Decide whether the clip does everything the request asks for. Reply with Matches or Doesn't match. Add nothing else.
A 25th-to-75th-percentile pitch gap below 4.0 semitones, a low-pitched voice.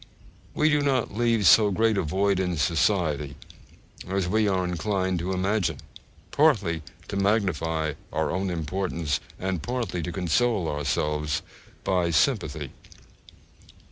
Doesn't match